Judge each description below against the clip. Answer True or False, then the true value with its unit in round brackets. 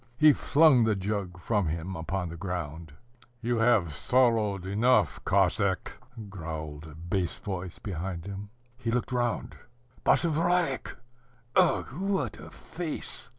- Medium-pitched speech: False (100 Hz)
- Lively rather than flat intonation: True (6.1 semitones)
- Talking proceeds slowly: True (125 wpm)